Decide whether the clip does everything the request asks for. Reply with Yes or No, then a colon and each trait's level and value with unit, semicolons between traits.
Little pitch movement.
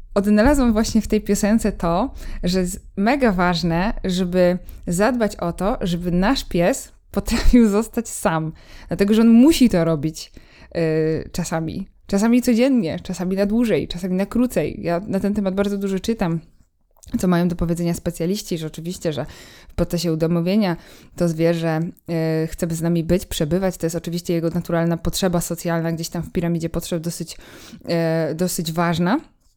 No: average, 3.4 semitones